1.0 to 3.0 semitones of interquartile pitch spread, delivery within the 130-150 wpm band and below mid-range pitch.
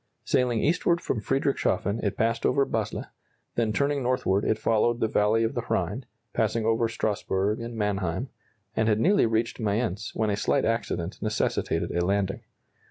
No: narrow, 2.4 semitones; average, 165 wpm; low, 110 Hz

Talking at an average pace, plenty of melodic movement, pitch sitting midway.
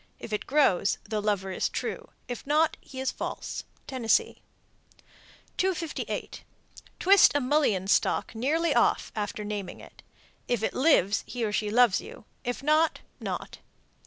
No: average, 145 wpm; wide, 6.1 semitones; high, 245 Hz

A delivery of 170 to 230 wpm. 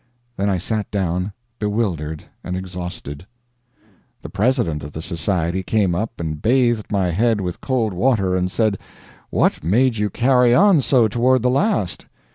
No: average, 155 wpm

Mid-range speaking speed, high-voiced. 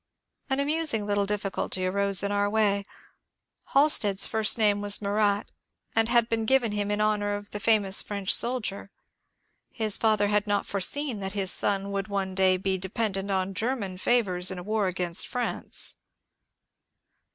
Yes: average, 160 wpm; high, 205 Hz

